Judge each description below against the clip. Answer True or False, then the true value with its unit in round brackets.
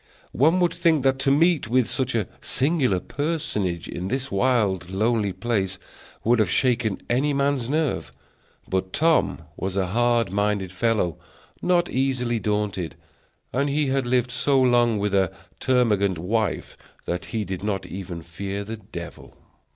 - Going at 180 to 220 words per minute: False (150 wpm)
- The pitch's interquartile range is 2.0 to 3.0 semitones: False (5.6 semitones)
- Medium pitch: False (115 Hz)